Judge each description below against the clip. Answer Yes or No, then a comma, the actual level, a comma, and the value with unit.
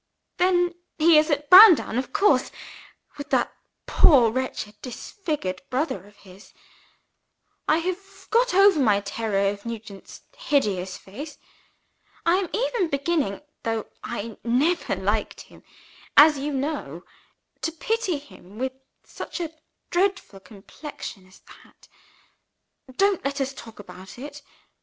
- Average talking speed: No, slow, 130 wpm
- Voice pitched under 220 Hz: No, very high, 275 Hz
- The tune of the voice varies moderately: No, wide, 8.4 semitones